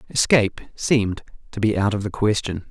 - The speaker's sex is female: No, male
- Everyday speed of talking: Yes, average, 180 wpm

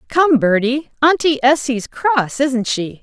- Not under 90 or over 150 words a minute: Yes, average, 140 wpm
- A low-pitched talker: No, very high, 265 Hz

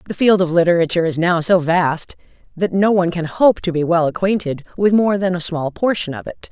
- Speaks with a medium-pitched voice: Yes, medium, 175 Hz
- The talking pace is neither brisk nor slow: No, fast, 230 wpm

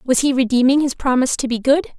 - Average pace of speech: No, fast, 240 wpm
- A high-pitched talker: Yes, very high, 260 Hz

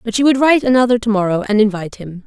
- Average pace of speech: No, fast, 265 wpm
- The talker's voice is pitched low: No, high, 220 Hz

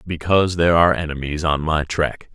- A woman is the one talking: No, male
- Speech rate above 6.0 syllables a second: No, 5.9 syllables/s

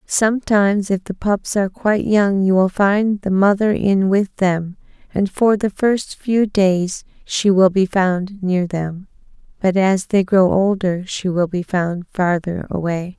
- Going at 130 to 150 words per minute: No, average, 175 wpm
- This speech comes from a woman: Yes, female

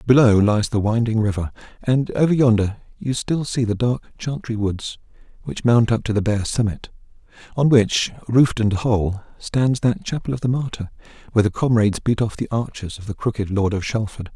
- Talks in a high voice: No, low, 115 Hz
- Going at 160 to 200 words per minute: Yes, average, 190 wpm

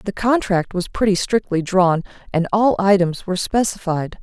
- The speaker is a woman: Yes, female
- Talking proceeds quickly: No, average, 155 wpm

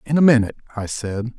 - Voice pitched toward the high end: No, low, 120 Hz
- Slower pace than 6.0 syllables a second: No, 6.7 syllables/s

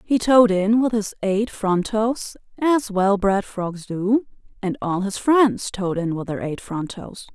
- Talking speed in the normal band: Yes, average, 195 wpm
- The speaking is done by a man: No, female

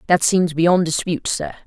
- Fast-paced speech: No, average, 180 wpm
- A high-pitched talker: No, medium, 170 Hz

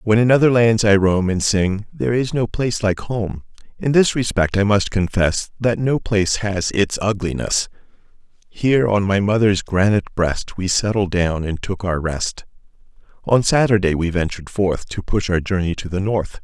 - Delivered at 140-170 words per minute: No, average, 185 wpm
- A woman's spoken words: No, male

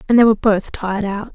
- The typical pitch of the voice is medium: No, high, 210 Hz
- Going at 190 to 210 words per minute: No, fast, 265 wpm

